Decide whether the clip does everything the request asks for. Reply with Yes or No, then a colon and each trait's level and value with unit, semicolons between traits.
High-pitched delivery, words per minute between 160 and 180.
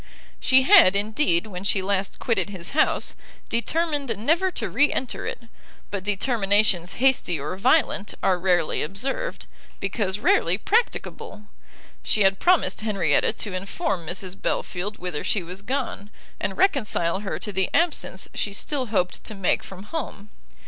No: high, 205 Hz; average, 150 wpm